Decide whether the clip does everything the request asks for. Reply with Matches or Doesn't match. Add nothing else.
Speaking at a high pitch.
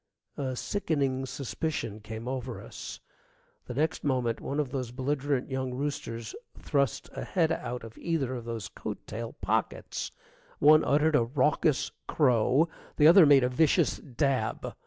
Doesn't match